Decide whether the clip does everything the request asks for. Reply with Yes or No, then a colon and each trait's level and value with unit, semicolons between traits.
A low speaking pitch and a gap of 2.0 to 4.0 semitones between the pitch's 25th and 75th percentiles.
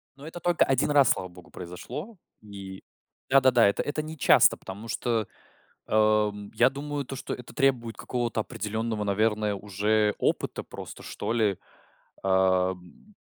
No: low, 110 Hz; average, 4.9 semitones